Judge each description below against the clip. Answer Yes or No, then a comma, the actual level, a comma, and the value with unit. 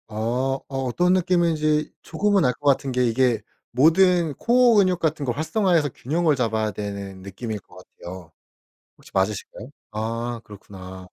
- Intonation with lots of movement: Yes, wide, 7.4 semitones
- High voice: No, low, 130 Hz